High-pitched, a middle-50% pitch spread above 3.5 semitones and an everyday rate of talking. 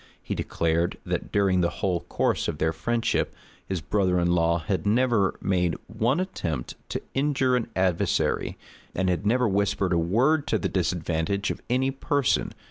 No: very low, 95 Hz; wide, 5.5 semitones; average, 165 wpm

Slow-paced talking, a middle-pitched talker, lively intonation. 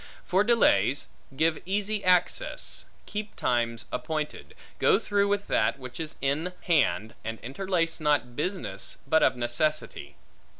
Yes: slow, 130 wpm; medium, 155 Hz; wide, 7.3 semitones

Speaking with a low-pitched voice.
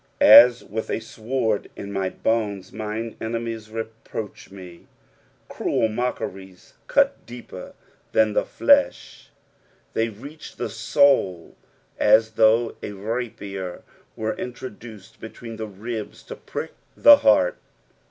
Yes: low, 110 Hz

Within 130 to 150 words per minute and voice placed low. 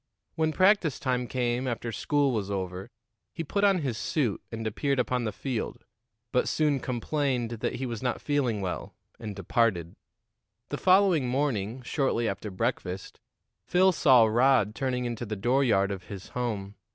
No: average, 160 wpm; low, 125 Hz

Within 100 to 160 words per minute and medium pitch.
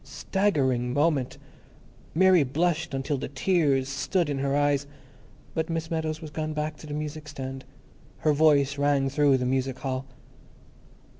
Yes: average, 150 wpm; medium, 145 Hz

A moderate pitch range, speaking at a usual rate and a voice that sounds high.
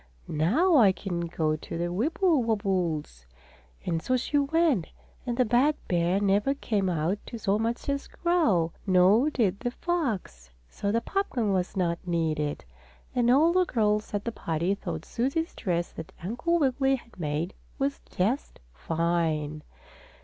No: wide, 7.5 semitones; average, 150 wpm; high, 205 Hz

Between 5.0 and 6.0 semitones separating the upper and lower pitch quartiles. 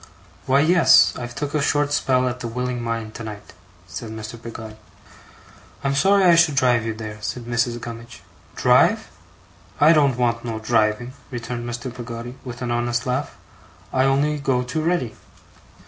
No: average, 2.8 semitones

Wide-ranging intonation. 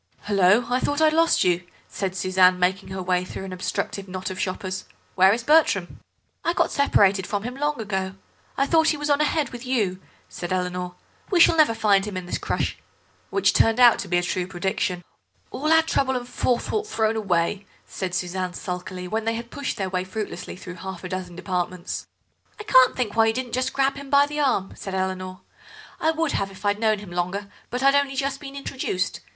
Yes: wide, 6.2 semitones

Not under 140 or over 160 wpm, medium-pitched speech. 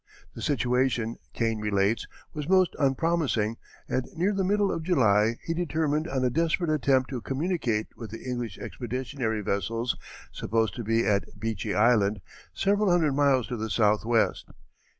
No: average, 150 wpm; low, 125 Hz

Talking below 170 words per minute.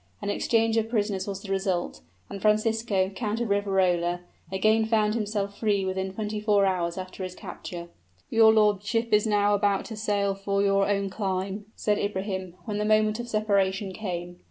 No: average, 175 wpm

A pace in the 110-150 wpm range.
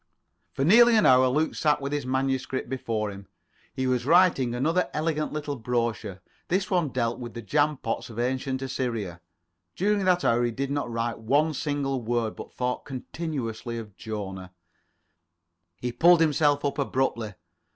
No: average, 160 wpm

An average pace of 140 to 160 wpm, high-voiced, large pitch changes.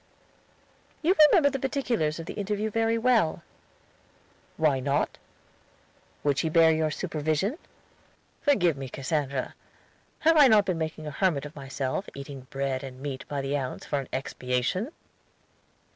No: average, 145 wpm; medium, 155 Hz; wide, 7.4 semitones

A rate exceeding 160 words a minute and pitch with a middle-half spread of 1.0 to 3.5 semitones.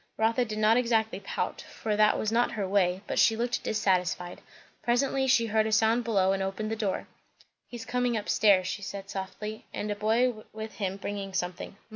Yes: average, 195 wpm; average, 2.7 semitones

